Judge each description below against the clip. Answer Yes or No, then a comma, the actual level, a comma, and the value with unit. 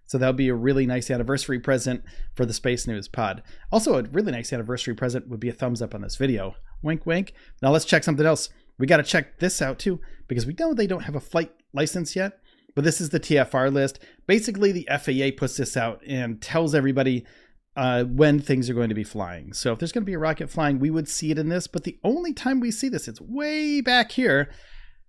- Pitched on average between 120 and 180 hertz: Yes, medium, 140 Hz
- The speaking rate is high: Yes, fast, 240 wpm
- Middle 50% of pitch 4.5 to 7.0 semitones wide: Yes, average, 5.1 semitones